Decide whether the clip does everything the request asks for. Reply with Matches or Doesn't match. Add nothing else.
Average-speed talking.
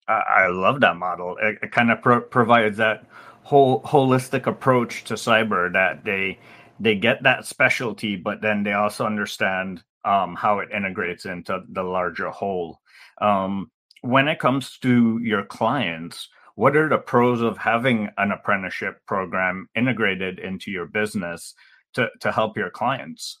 Matches